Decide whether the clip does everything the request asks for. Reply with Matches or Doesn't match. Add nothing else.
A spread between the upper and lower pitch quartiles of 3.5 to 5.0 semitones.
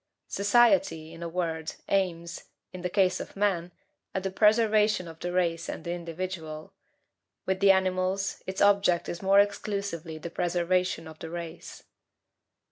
Doesn't match